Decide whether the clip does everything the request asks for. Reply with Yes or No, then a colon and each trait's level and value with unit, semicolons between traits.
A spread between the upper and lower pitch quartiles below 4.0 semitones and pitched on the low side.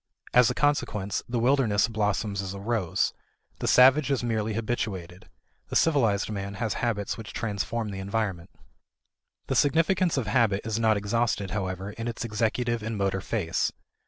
Yes: average, 3.1 semitones; low, 110 Hz